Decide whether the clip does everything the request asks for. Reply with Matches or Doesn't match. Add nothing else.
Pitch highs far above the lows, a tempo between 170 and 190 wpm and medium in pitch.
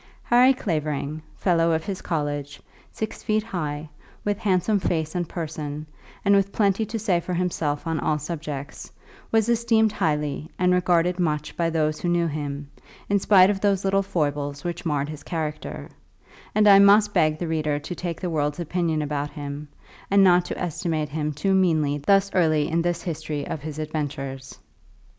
Doesn't match